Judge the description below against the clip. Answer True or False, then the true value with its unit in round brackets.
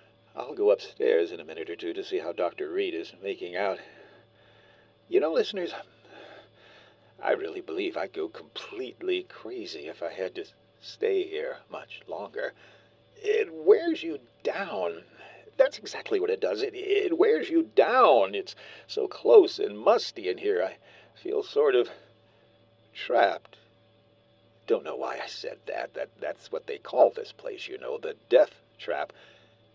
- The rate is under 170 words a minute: True (155 wpm)